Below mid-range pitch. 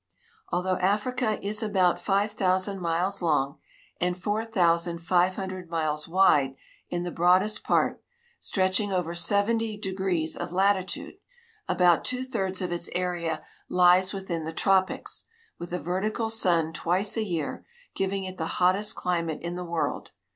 No: medium, 185 Hz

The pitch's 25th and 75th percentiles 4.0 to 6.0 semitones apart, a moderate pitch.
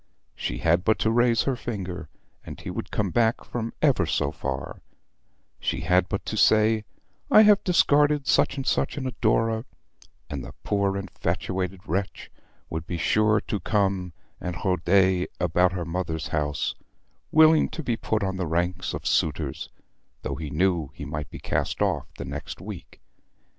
No: average, 5.2 semitones; very low, 95 Hz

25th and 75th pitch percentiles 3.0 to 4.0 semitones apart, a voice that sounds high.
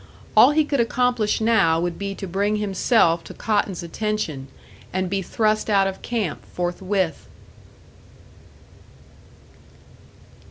Yes: average, 3.6 semitones; high, 200 Hz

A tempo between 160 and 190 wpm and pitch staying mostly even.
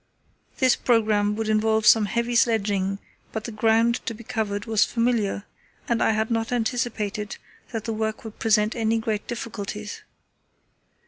No: average, 150 wpm; narrow, 1.5 semitones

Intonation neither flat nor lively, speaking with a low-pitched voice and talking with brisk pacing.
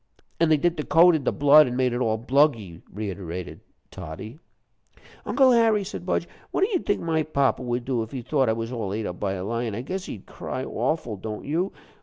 No: wide, 6.4 semitones; low, 125 Hz; fast, 225 wpm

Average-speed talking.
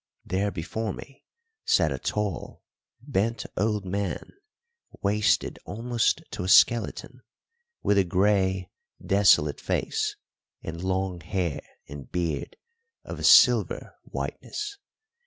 No: slow, 110 wpm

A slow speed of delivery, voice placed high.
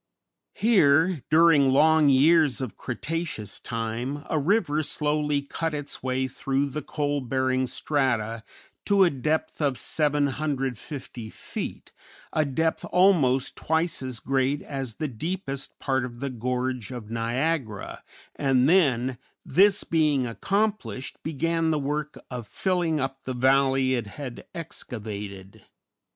No: slow, 125 wpm; medium, 140 Hz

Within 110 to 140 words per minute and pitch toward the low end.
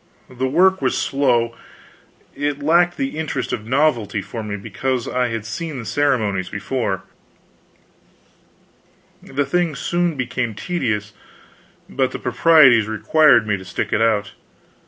Yes: slow, 135 wpm; low, 125 Hz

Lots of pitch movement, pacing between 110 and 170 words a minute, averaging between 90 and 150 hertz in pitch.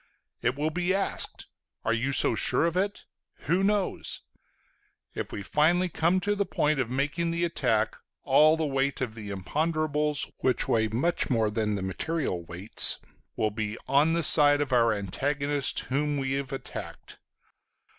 Yes: wide, 5.9 semitones; average, 165 wpm; medium, 140 Hz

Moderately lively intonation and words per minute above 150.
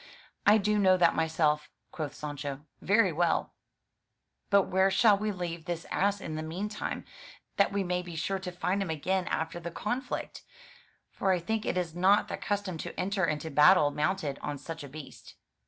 Yes: average, 3.7 semitones; average, 190 wpm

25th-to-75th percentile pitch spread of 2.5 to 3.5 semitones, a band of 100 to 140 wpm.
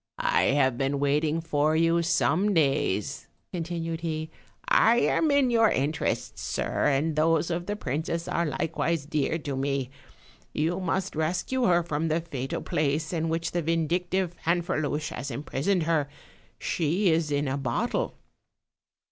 No: average, 2.8 semitones; average, 150 wpm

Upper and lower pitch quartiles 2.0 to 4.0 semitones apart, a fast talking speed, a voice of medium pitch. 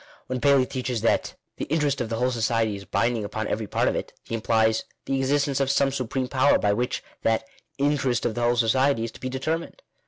No: average, 3.3 semitones; fast, 225 wpm; low, 125 Hz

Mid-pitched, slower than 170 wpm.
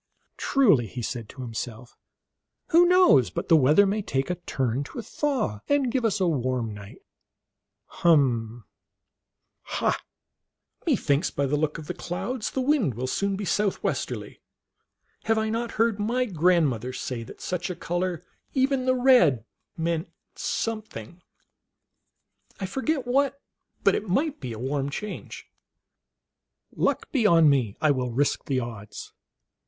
Yes: medium, 170 Hz; average, 150 wpm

